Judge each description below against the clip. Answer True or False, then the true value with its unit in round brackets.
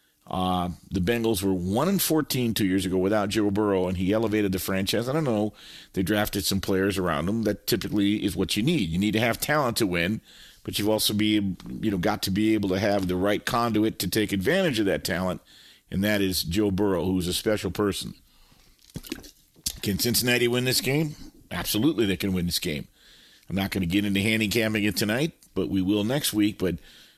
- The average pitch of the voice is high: False (105 Hz)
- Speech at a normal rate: False (210 wpm)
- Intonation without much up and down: True (2.3 semitones)